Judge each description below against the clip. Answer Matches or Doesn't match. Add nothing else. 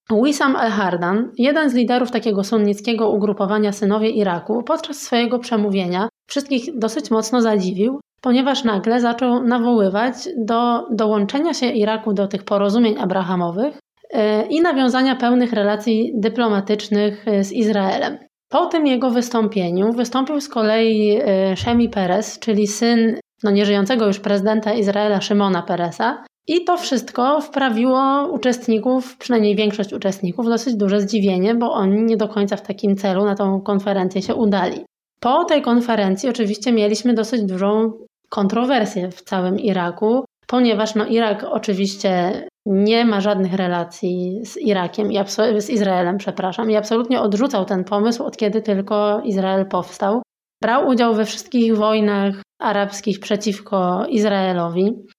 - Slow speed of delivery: Doesn't match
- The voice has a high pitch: Matches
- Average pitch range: Matches